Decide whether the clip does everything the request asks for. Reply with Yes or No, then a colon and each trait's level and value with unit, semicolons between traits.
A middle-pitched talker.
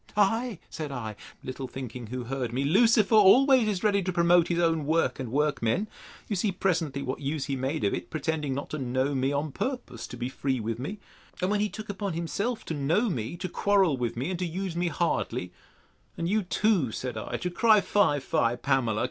Yes: medium, 160 Hz